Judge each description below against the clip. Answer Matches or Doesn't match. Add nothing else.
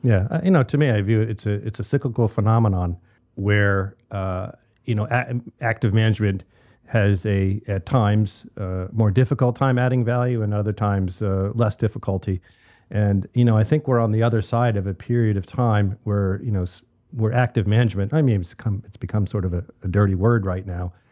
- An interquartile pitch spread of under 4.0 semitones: Matches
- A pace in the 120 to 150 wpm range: Doesn't match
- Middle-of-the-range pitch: Doesn't match